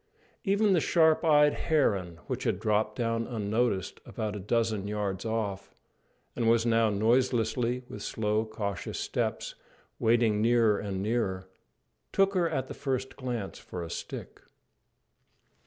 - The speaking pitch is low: Yes, low, 115 Hz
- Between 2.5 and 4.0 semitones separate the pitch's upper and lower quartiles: Yes, average, 3.4 semitones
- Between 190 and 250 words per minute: No, average, 140 wpm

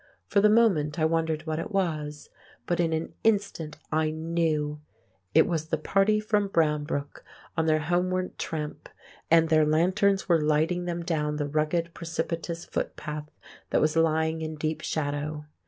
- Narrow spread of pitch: Yes, narrow, 2.2 semitones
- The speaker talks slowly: No, average, 155 wpm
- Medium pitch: Yes, medium, 160 Hz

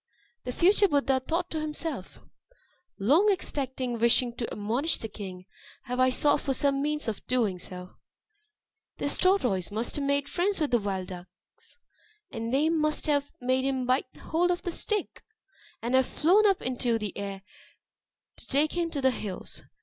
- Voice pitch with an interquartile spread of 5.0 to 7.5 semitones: Yes, average, 5.3 semitones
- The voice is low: No, very high, 260 Hz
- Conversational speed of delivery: Yes, average, 170 wpm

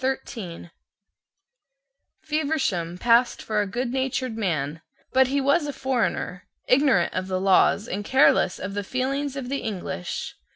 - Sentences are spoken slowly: Yes, slow, 130 wpm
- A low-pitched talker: No, high, 240 Hz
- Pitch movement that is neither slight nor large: No, wide, 6.1 semitones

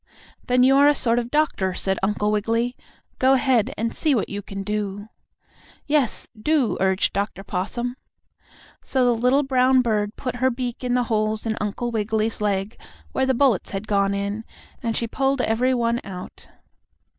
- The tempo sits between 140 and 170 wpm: No, average, 180 wpm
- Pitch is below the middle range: No, high, 230 Hz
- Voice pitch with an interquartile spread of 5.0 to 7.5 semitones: No, average, 3.6 semitones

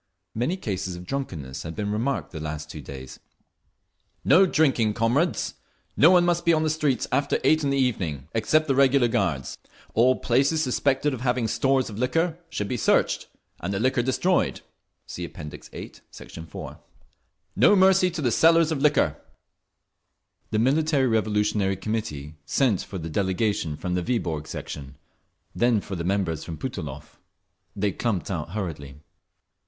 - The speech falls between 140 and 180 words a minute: Yes, average, 160 wpm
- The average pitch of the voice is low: Yes, low, 115 Hz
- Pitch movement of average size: No, wide, 7.6 semitones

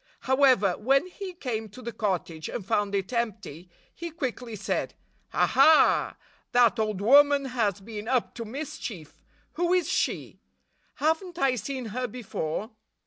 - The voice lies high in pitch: Yes, high, 240 Hz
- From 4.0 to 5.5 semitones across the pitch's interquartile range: Yes, average, 5.1 semitones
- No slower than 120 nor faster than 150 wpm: Yes, average, 145 wpm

